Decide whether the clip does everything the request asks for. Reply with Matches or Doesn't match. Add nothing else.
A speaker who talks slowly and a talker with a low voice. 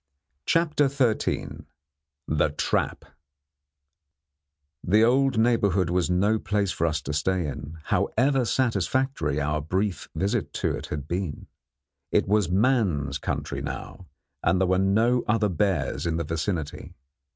Matches